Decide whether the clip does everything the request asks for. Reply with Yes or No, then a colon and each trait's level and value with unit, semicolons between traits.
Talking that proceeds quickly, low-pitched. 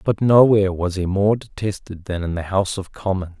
Yes: fast, 210 wpm; very low, 95 Hz